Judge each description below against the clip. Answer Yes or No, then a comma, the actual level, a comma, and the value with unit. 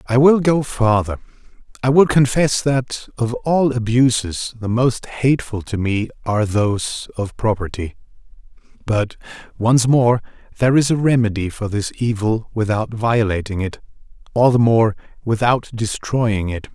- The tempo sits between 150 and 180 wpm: No, average, 140 wpm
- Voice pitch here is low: Yes, low, 115 Hz